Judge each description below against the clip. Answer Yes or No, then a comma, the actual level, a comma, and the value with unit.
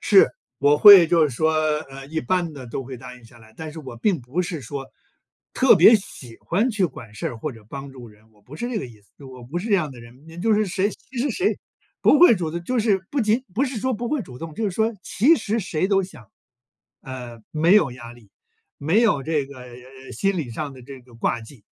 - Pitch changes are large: Yes, wide, 8.0 semitones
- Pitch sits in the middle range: Yes, medium, 155 Hz